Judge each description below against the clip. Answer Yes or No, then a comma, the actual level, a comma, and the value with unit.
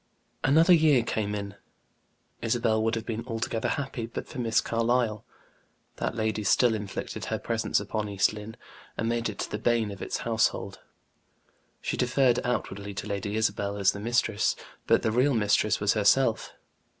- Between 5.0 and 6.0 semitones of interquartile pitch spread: No, narrow, 2.5 semitones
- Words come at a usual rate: Yes, average, 160 wpm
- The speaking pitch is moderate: No, low, 110 Hz